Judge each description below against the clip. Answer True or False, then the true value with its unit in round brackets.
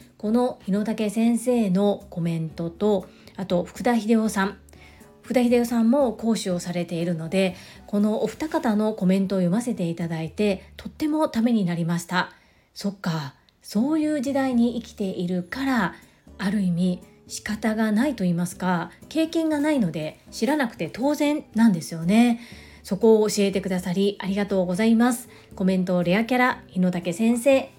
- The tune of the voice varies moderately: True (4.6 semitones)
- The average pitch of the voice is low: False (210 Hz)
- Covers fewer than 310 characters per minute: False (340 characters per minute)